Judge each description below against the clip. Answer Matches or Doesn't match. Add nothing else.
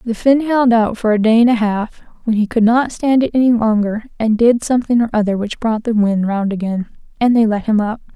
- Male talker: Doesn't match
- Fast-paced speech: Matches